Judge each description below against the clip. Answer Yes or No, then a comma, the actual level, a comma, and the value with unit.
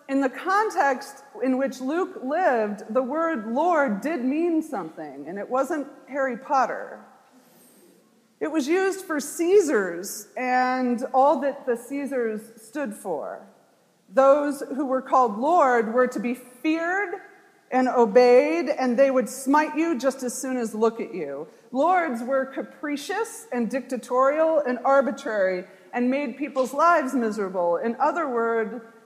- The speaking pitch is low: No, very high, 265 Hz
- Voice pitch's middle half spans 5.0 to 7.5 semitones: No, average, 3.8 semitones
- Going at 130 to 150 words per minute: Yes, average, 140 wpm